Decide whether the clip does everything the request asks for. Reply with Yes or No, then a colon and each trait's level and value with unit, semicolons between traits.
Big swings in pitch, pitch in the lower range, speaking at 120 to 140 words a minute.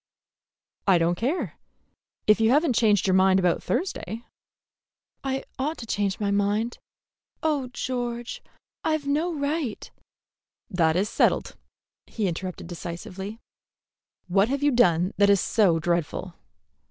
No: wide, 5.8 semitones; high, 210 Hz; slow, 135 wpm